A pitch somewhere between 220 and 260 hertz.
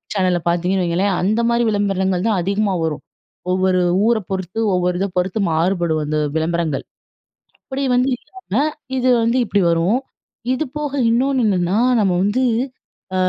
No: high, 190 Hz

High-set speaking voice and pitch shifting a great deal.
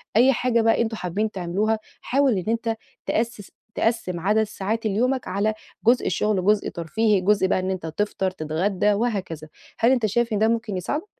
No: high, 215 Hz; average, 3.4 semitones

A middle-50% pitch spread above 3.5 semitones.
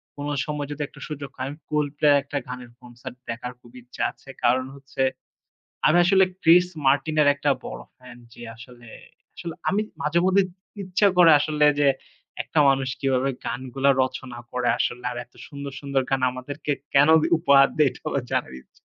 No: average, 3.0 semitones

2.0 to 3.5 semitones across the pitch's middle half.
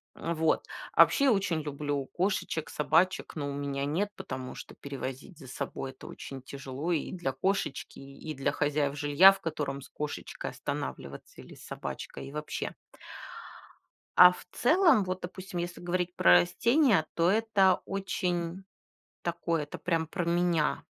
No: average, 4.5 semitones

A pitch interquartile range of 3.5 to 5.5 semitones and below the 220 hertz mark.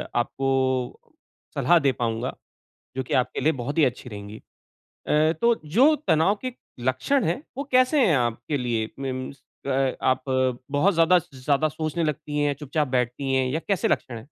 Yes: average, 3.9 semitones; medium, 140 Hz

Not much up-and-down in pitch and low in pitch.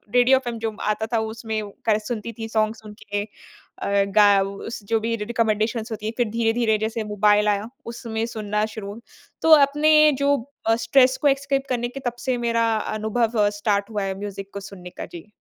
No: narrow, 2.2 semitones; high, 220 Hz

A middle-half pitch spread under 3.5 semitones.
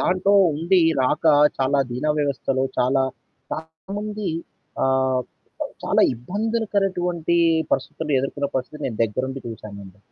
No: wide, 5.5 semitones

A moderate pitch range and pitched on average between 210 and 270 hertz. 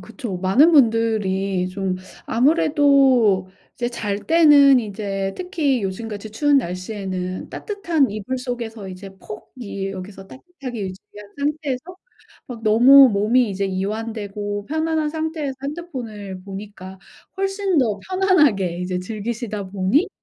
No: wide, 6.4 semitones; high, 225 Hz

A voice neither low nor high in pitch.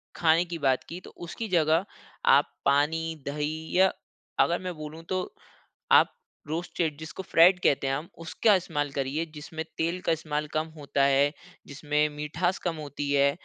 Yes: medium, 160 Hz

